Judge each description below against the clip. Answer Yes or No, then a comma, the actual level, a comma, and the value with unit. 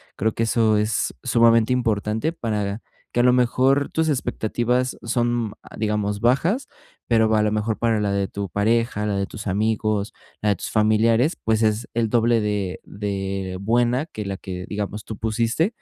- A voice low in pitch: Yes, low, 110 Hz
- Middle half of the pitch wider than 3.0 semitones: No, narrow, 2.4 semitones